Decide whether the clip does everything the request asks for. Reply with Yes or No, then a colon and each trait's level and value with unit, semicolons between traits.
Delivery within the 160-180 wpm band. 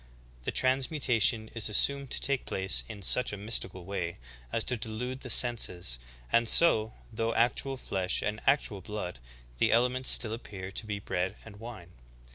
Yes: average, 165 wpm